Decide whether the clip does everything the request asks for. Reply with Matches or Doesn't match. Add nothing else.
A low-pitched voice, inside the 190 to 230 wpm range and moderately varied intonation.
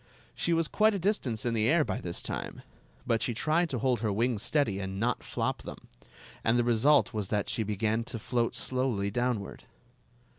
Matches